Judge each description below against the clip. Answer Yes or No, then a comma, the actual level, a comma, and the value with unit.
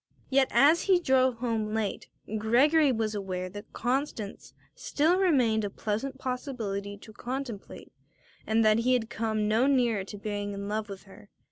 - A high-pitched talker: Yes, high, 225 Hz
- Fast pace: No, average, 160 wpm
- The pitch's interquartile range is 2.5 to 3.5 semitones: No, average, 4.1 semitones